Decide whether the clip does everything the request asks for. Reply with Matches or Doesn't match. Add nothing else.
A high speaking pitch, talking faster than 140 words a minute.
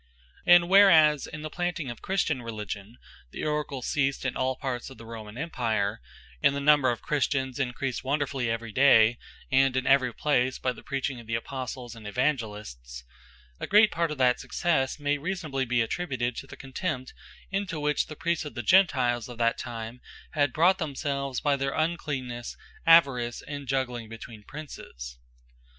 Doesn't match